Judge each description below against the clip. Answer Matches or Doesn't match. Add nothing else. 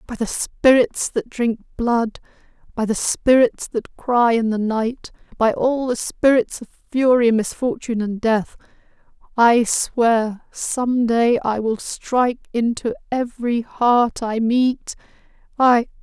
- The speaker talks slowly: Matches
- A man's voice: Doesn't match